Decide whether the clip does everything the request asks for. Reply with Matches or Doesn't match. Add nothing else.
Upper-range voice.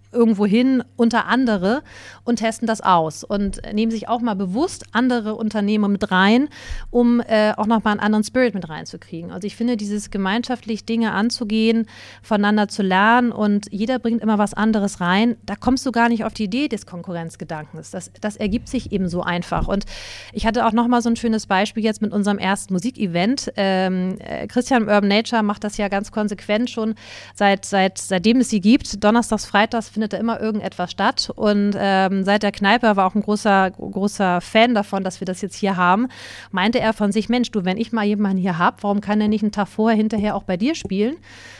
Matches